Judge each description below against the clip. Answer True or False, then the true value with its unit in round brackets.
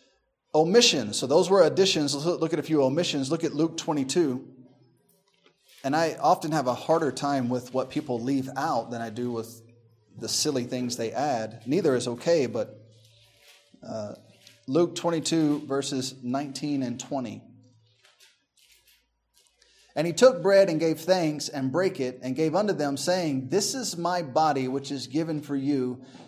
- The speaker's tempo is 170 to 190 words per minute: False (160 wpm)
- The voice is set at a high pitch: False (140 Hz)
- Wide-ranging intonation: False (4.4 semitones)